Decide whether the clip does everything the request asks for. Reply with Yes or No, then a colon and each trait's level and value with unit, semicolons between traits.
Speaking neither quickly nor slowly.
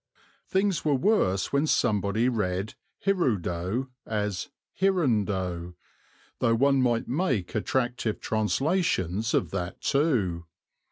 No: slow, 100 wpm